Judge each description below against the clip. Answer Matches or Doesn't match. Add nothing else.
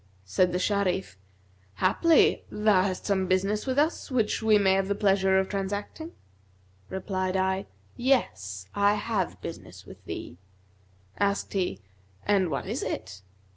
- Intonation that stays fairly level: Matches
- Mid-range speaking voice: Doesn't match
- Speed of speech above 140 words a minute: Doesn't match